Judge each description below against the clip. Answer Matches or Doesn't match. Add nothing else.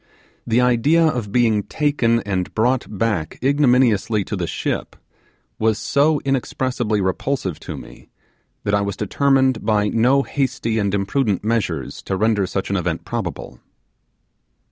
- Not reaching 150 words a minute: Matches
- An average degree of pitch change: Matches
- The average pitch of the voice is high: Doesn't match